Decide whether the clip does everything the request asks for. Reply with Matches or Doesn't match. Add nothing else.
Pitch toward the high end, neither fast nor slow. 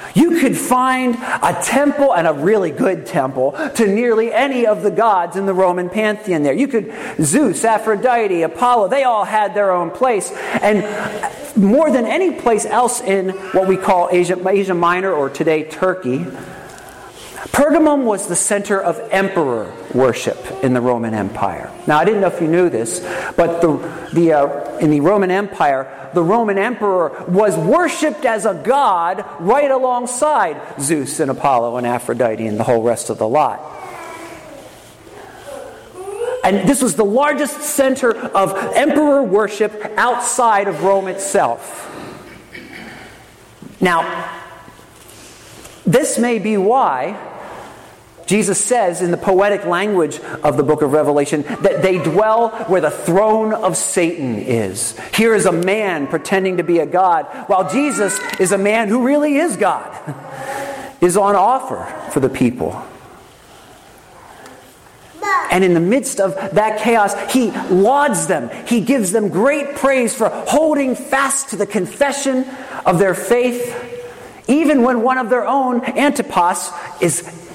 Matches